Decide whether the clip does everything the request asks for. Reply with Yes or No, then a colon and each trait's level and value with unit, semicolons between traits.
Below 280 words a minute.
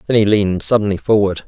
Yes: fast, 205 wpm